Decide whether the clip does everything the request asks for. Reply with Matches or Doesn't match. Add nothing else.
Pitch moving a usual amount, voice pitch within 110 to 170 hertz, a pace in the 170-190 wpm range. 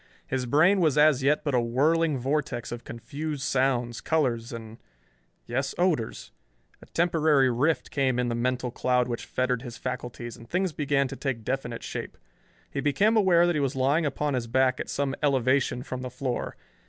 Matches